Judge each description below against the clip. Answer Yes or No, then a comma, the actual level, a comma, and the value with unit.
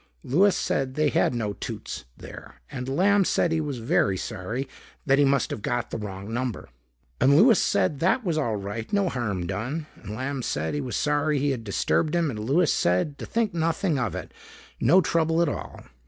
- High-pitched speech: No, low, 135 Hz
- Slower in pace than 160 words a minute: No, average, 200 wpm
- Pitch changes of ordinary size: No, wide, 6.4 semitones